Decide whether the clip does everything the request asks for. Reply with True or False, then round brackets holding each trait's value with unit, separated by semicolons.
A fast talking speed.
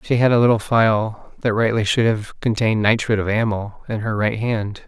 True (210 wpm)